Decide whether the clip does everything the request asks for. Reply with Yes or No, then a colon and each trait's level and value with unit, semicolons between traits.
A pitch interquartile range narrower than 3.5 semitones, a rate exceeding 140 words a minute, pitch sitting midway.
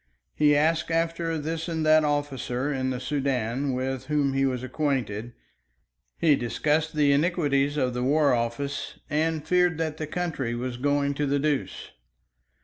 Yes: average, 3.1 semitones; average, 155 wpm; medium, 145 Hz